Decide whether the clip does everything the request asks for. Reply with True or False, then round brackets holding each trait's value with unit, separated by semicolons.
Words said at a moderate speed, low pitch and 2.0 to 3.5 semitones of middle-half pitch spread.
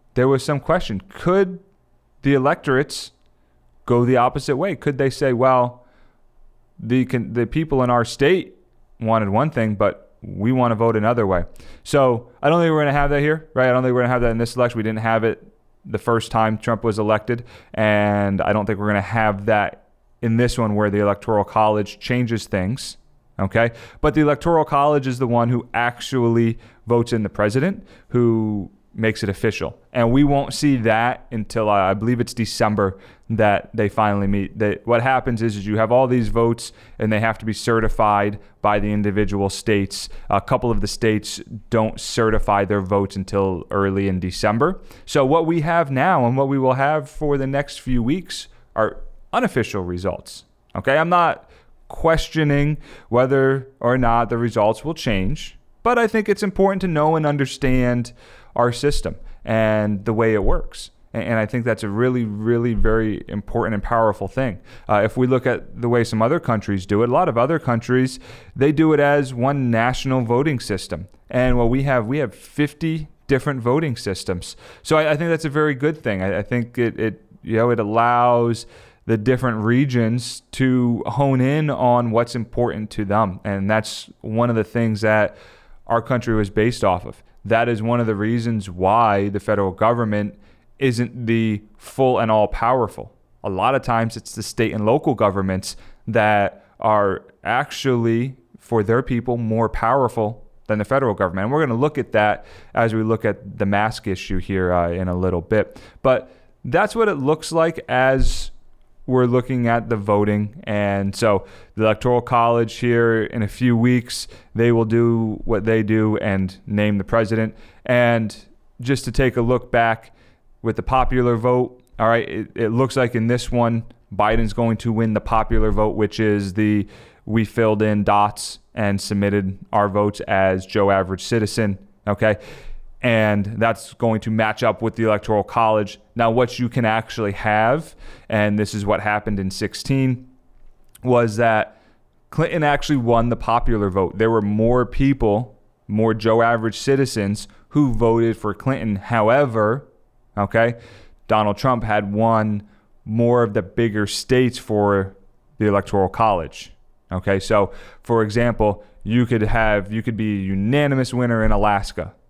True (180 wpm; 115 Hz; 3.0 semitones)